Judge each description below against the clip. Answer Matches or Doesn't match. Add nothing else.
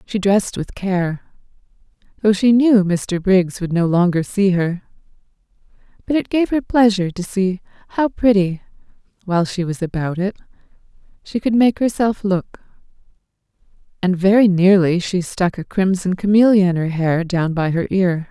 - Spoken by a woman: Matches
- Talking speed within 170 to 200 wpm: Doesn't match